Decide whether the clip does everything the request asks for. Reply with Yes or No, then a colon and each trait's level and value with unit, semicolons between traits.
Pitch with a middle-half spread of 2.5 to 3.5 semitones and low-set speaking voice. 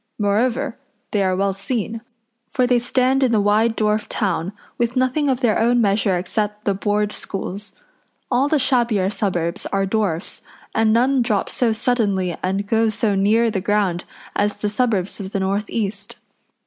No: average, 3.2 semitones; high, 210 Hz